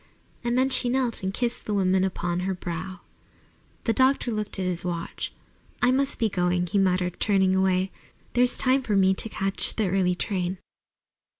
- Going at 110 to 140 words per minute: No, average, 180 wpm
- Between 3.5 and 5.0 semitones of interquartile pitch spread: Yes, average, 4.4 semitones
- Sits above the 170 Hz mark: Yes, high, 190 Hz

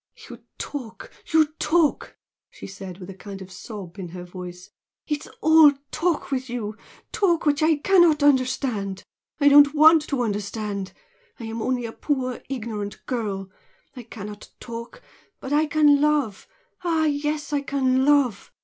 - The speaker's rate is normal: Yes, average, 160 wpm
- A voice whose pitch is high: Yes, very high, 255 Hz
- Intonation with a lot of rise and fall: Yes, wide, 6.3 semitones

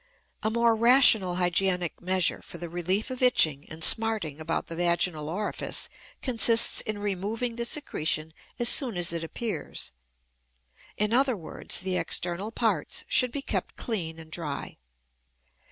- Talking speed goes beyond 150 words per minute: No, average, 145 wpm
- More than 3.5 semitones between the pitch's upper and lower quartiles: Yes, wide, 5.4 semitones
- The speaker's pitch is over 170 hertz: Yes, high, 190 Hz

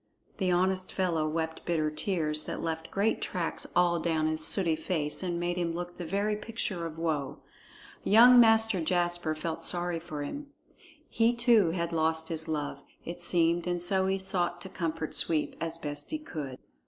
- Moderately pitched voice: Yes, medium, 170 Hz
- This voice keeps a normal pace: Yes, average, 180 wpm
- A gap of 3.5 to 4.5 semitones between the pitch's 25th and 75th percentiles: No, average, 2.8 semitones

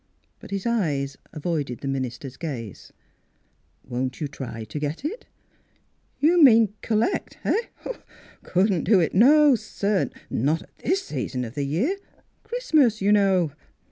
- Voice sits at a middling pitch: Yes, medium, 180 Hz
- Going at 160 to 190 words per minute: No, average, 150 wpm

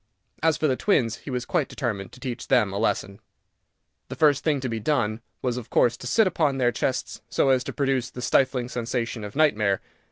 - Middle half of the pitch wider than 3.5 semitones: No, average, 3.2 semitones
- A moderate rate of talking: No, fast, 215 wpm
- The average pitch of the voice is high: No, low, 125 Hz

